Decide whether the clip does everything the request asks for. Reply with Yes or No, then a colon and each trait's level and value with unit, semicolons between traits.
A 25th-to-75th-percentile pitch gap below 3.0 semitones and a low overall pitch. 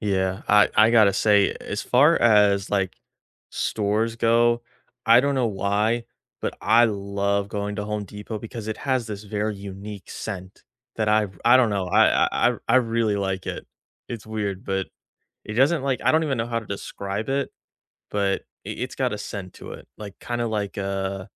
Yes: narrow, 2.6 semitones; low, 105 Hz